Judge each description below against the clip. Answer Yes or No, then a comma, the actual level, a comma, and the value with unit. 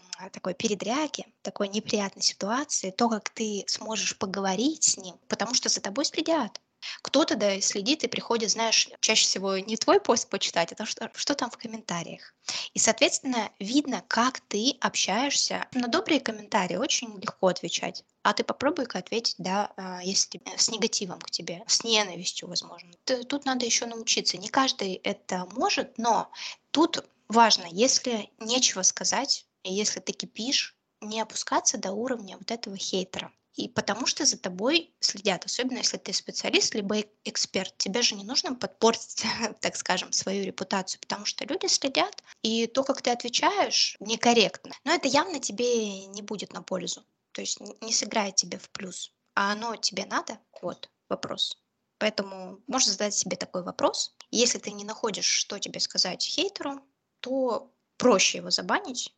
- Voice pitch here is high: Yes, high, 225 Hz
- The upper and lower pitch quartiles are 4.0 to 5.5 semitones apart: Yes, average, 4.5 semitones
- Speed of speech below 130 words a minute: No, average, 155 wpm